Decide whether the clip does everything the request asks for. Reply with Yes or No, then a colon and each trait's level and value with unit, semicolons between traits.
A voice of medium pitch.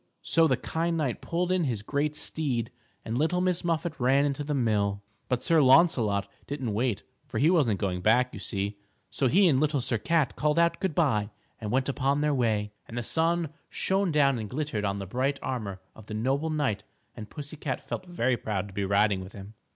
No: low, 130 Hz